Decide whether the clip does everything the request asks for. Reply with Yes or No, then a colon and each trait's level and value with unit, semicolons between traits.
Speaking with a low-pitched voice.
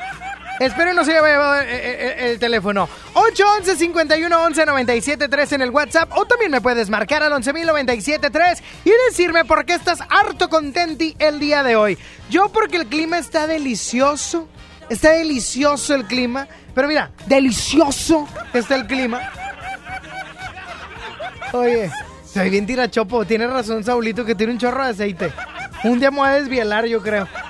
No: very high, 285 Hz